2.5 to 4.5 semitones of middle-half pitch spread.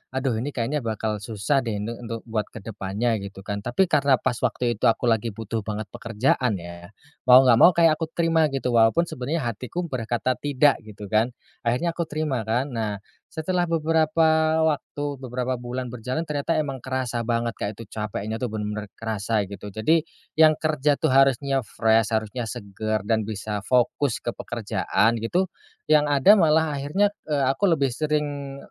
No: average, 4.9 semitones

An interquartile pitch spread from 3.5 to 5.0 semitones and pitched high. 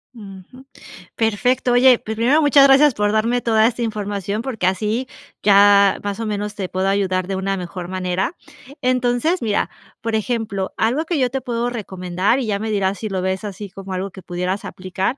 Yes: average, 4.1 semitones; high, 210 Hz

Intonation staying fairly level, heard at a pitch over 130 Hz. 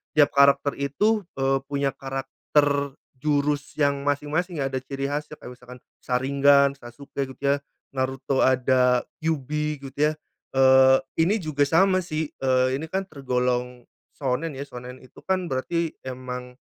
Yes: narrow, 2.3 semitones; medium, 140 Hz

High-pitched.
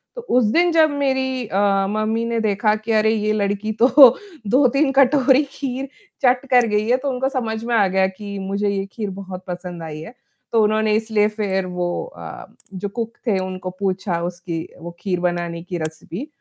Yes: high, 215 Hz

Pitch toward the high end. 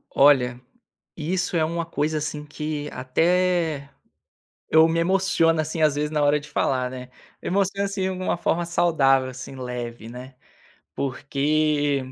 No: medium, 150 Hz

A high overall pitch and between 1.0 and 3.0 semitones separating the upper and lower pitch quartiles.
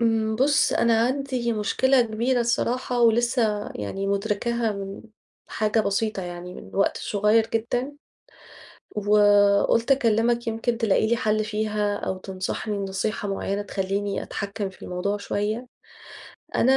Yes: high, 215 Hz; average, 2.7 semitones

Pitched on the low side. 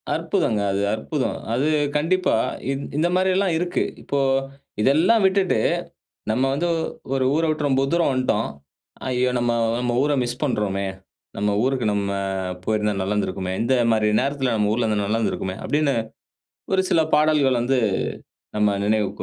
Yes: low, 130 Hz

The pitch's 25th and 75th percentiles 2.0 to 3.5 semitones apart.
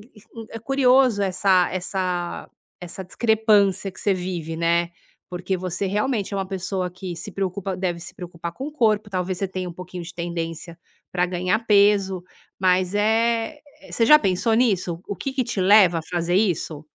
Yes: average, 3.0 semitones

